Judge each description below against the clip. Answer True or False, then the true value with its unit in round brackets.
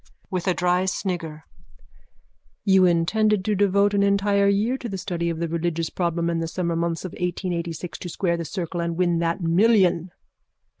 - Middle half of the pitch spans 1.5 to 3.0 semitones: True (2.7 semitones)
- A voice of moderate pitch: True (180 Hz)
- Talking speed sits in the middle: True (180 wpm)